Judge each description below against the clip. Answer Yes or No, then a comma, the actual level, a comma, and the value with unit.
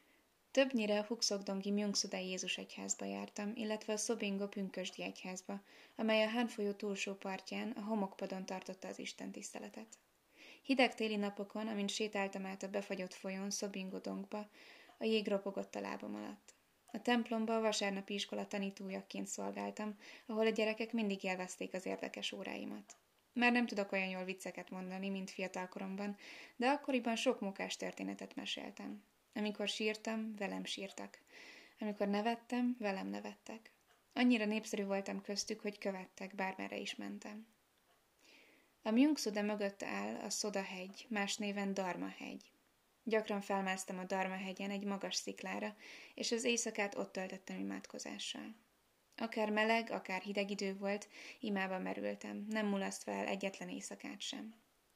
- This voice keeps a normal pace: Yes, average, 135 wpm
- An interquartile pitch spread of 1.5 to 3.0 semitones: Yes, narrow, 2.5 semitones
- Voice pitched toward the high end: Yes, high, 200 Hz